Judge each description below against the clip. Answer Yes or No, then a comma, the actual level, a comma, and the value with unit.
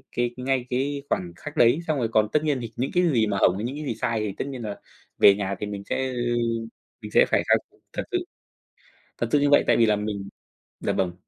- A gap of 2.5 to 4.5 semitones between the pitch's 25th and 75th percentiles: No, average, 5.2 semitones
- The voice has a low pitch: Yes, low, 120 Hz